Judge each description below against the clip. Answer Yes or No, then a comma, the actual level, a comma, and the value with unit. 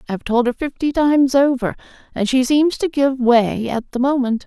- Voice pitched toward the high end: Yes, very high, 260 Hz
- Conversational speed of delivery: No, fast, 215 wpm